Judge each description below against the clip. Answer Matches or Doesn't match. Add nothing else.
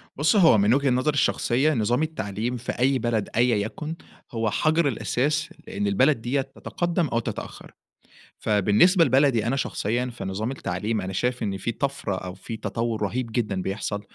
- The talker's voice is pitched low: Matches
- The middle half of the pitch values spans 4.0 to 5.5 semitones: Matches